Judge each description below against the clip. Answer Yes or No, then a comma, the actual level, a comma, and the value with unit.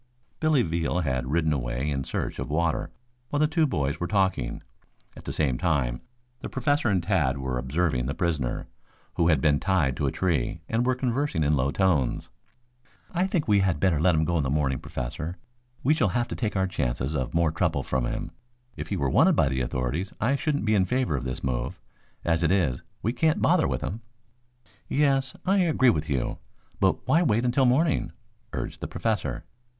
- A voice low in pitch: Yes, very low, 85 Hz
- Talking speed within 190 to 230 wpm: Yes, average, 200 wpm